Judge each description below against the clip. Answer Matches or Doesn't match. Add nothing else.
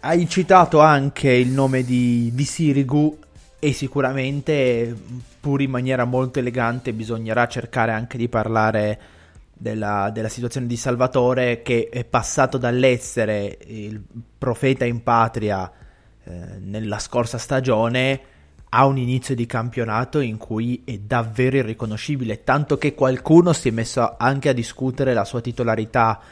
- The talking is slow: Doesn't match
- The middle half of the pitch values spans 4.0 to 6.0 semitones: Doesn't match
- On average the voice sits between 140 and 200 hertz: Doesn't match